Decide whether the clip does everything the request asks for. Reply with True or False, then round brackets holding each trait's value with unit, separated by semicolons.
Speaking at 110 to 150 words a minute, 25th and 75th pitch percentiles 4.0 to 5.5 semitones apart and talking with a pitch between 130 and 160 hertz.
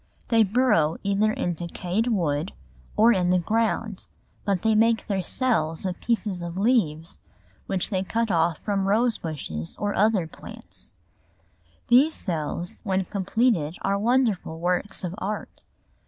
False (140 wpm; 4.4 semitones; 195 Hz)